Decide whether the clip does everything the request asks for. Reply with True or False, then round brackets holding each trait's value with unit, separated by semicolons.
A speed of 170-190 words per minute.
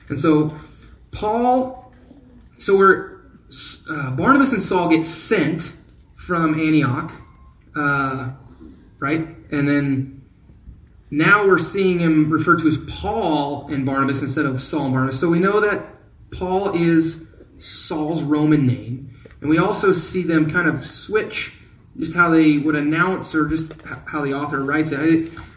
False (145 wpm)